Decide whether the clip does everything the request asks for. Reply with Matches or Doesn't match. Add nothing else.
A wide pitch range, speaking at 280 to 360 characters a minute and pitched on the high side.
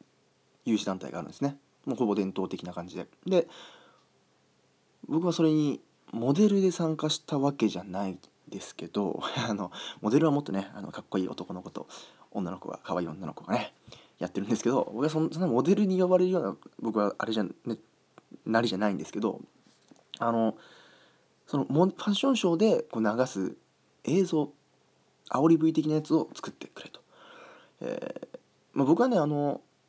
Doesn't match